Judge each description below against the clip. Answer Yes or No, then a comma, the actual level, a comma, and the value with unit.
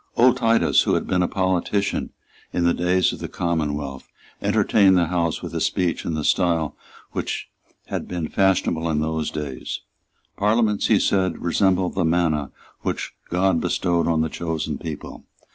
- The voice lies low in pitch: Yes, very low, 85 Hz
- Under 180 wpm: Yes, average, 160 wpm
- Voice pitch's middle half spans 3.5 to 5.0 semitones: No, average, 2.8 semitones